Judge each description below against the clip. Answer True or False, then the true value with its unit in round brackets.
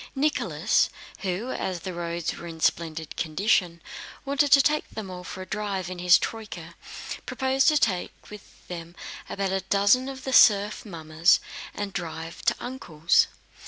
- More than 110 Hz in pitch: True (190 Hz)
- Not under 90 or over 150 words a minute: False (160 wpm)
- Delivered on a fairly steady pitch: False (4.7 semitones)